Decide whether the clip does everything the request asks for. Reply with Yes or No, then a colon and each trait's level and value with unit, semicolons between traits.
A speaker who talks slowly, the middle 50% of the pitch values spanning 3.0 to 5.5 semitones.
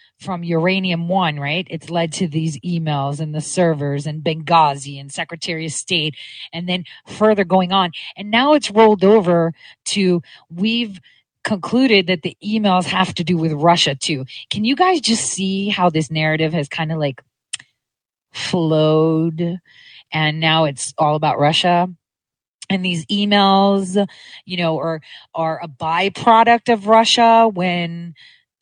No: average, 150 wpm; average, 3.5 semitones